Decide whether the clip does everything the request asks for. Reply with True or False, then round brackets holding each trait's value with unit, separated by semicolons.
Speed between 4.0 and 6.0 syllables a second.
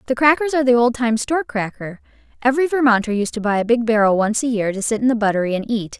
False (6.9 syllables/s)